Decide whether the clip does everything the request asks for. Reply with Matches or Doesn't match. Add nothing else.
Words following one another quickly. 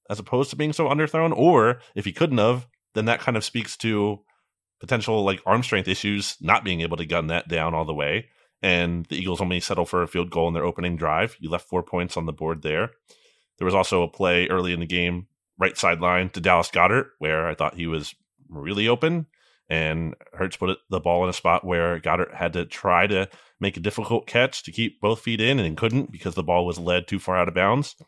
Matches